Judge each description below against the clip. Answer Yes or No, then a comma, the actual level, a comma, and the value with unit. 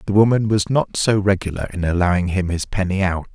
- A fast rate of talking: Yes, fast, 215 wpm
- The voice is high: No, very low, 95 Hz